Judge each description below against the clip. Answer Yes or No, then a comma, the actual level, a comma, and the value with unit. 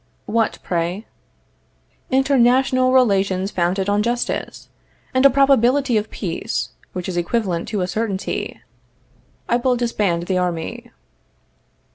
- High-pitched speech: Yes, high, 215 Hz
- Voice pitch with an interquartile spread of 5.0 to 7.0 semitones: Yes, average, 5.3 semitones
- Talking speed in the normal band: No, slow, 115 wpm